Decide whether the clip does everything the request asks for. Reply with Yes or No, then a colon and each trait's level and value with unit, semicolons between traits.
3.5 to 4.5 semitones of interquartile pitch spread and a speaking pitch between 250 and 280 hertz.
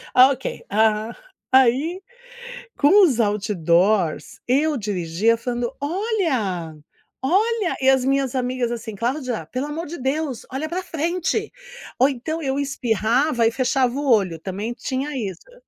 No: average, 5.2 semitones; very high, 255 Hz